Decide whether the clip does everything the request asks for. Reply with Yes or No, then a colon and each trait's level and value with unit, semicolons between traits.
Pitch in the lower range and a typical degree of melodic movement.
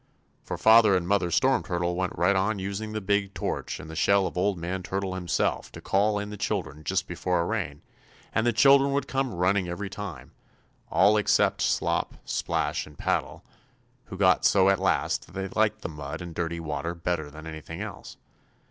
Yes: very low, 95 Hz; average, 3.2 semitones